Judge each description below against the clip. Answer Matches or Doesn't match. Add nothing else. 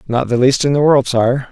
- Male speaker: Matches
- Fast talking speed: Matches